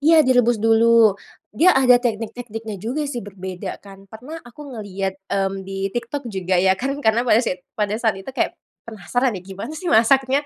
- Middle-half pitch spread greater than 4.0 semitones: Yes, average, 4.5 semitones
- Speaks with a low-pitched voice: No, high, 225 Hz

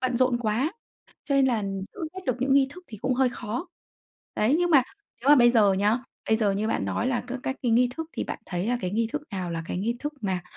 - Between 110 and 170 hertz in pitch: No, high, 240 Hz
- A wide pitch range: No, average, 4.0 semitones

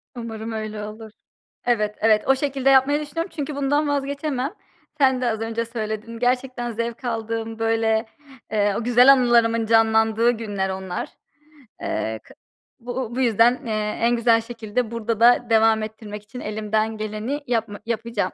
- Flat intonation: Yes, narrow, 2.3 semitones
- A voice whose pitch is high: Yes, high, 230 Hz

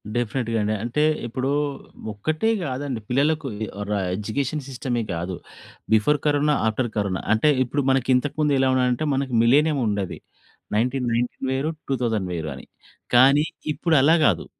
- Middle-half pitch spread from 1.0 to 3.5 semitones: No, average, 4.2 semitones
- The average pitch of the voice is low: Yes, low, 130 Hz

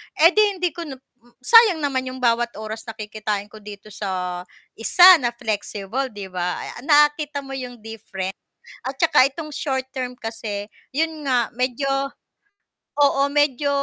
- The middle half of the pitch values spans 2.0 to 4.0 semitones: No, average, 5.1 semitones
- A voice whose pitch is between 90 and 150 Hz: No, very high, 255 Hz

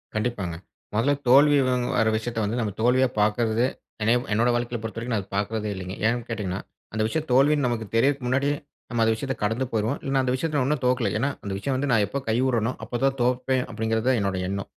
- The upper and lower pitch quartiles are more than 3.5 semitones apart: No, average, 3.2 semitones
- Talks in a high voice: No, low, 120 Hz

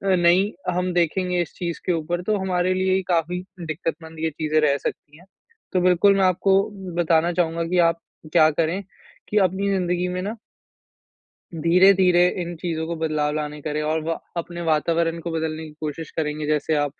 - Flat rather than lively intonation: Yes, narrow, 2.3 semitones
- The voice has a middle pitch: Yes, medium, 170 Hz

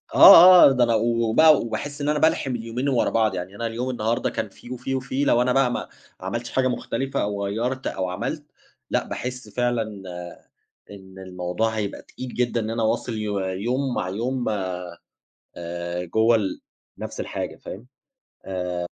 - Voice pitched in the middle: No, low, 115 Hz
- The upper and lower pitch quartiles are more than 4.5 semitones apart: No, average, 4.1 semitones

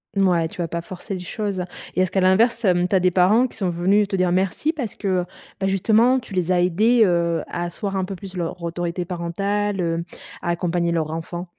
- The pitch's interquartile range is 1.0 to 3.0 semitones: Yes, narrow, 2.4 semitones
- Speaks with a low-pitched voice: No, medium, 185 Hz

